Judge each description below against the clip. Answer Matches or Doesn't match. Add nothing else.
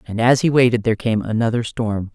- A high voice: Doesn't match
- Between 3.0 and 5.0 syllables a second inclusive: Doesn't match